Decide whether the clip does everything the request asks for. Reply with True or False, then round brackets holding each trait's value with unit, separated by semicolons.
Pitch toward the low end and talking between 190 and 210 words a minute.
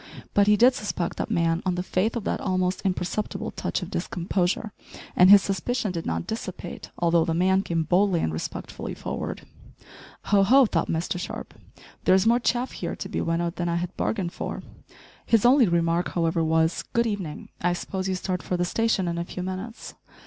False (185 Hz; 195 wpm)